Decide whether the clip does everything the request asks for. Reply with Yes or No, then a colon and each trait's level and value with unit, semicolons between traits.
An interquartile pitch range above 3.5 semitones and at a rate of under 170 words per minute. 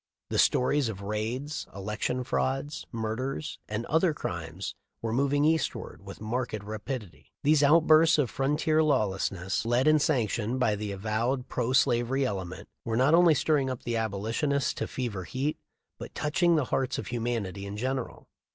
Yes: average, 5.1 semitones; average, 160 wpm